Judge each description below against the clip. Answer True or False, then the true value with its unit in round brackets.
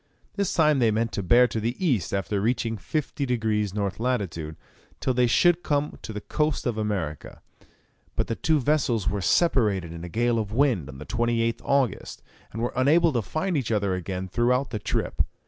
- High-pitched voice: False (115 Hz)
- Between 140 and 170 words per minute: False (195 wpm)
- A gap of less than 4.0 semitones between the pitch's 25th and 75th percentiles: False (5.0 semitones)